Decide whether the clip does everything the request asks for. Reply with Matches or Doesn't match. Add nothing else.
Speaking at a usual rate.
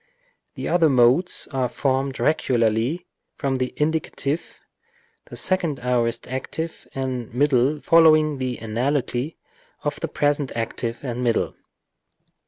Doesn't match